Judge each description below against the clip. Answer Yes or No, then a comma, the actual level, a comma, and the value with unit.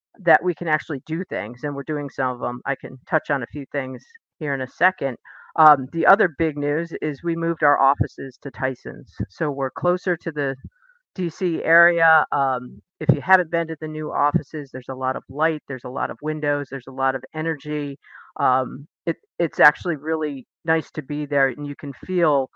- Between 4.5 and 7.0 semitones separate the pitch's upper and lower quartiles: No, average, 3.2 semitones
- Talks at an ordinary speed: No, fast, 210 wpm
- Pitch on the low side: No, medium, 150 Hz